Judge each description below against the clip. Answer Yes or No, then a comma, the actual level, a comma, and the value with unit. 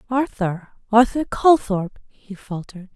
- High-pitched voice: Yes, high, 220 Hz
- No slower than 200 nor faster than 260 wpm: No, slow, 100 wpm